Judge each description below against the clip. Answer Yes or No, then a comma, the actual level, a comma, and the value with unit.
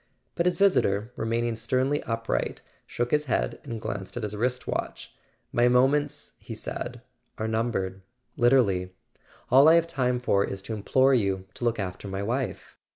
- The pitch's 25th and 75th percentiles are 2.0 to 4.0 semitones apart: No, average, 4.4 semitones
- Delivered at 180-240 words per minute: No, average, 155 wpm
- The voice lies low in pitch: Yes, low, 120 Hz